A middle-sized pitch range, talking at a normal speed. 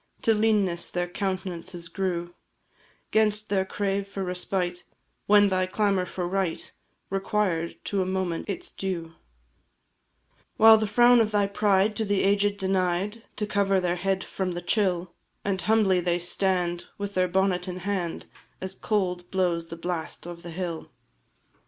No: narrow, 2.3 semitones; average, 150 wpm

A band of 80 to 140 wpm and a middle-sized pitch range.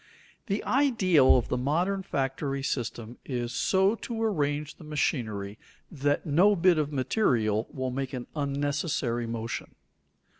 No: slow, 135 wpm; wide, 6.0 semitones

